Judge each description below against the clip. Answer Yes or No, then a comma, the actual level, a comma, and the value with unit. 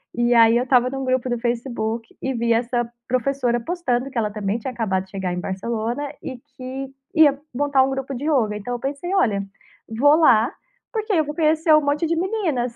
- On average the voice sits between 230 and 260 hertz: Yes, very high, 255 Hz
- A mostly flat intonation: No, average, 3.7 semitones